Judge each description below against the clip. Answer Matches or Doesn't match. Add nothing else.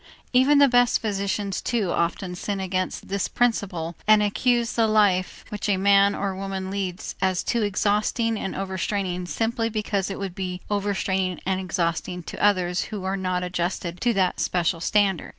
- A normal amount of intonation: Doesn't match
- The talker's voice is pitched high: Matches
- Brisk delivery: Doesn't match